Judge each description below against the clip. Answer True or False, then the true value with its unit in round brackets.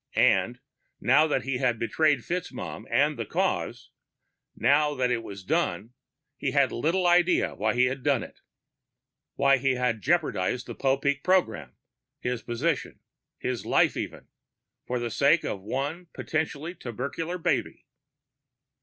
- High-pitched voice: False (135 Hz)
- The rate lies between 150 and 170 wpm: False (140 wpm)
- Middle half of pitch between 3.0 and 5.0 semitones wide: True (4.6 semitones)